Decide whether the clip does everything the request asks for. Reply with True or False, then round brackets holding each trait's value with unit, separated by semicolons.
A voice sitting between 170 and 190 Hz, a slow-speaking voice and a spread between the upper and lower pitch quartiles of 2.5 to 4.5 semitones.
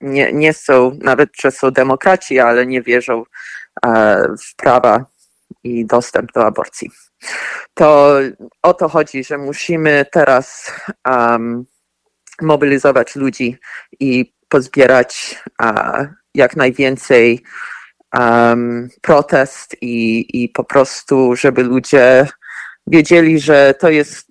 False (135 Hz; 105 wpm; 2.9 semitones)